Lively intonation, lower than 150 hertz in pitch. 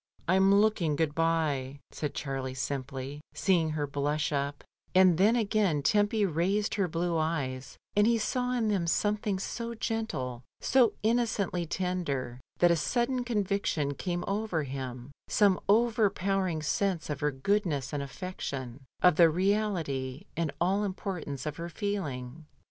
No: wide, 6.1 semitones; medium, 170 Hz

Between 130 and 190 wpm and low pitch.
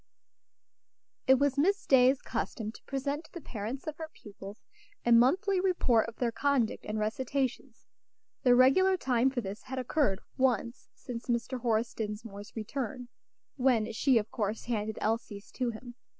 No: average, 155 wpm; high, 245 Hz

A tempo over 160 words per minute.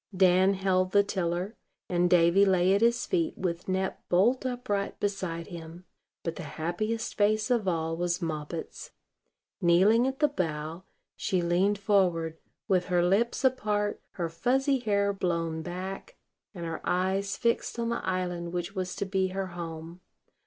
No: average, 155 wpm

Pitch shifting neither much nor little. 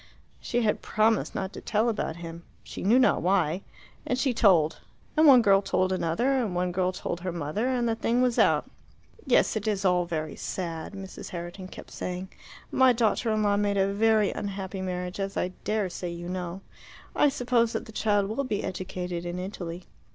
Yes: average, 3.8 semitones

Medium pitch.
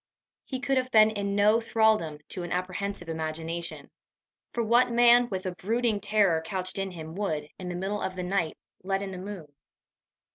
No: high, 195 Hz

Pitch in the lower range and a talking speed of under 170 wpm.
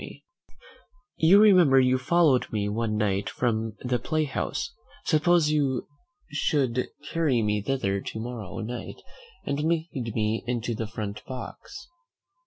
Yes: low, 125 Hz; slow, 135 wpm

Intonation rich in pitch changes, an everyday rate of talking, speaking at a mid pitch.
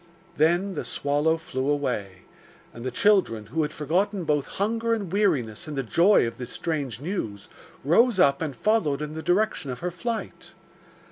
Yes: wide, 6.3 semitones; average, 175 wpm; medium, 155 Hz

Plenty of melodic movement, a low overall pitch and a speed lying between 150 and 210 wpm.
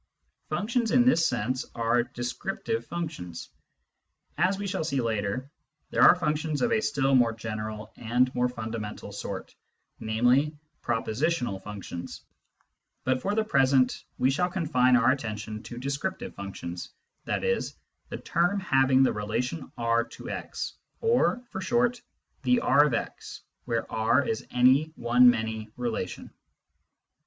No: wide, 6.0 semitones; low, 125 Hz; average, 140 wpm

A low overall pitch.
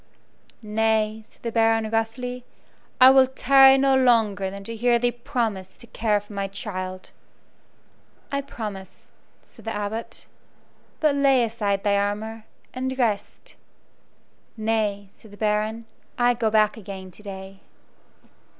No: high, 220 Hz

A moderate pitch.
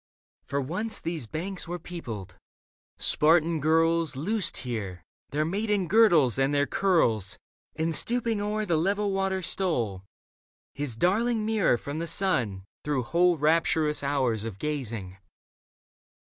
Yes: medium, 160 Hz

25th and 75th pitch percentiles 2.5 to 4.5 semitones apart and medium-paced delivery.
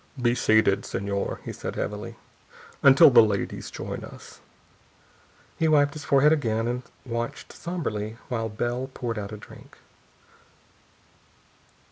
No: average, 4.0 semitones; slow, 125 wpm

